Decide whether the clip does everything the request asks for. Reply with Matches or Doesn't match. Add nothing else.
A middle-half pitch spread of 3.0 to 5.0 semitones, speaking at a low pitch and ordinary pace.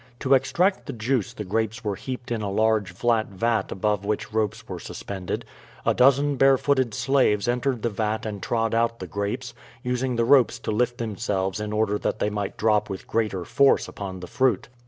Matches